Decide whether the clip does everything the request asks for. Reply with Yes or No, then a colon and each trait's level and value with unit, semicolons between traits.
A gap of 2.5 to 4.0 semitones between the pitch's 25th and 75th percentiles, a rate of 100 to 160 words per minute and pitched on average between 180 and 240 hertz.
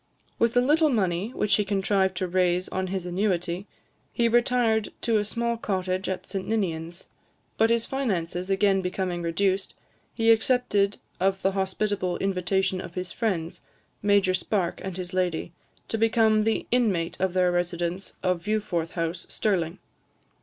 Yes: average, 3.1 semitones; average, 155 wpm; high, 190 Hz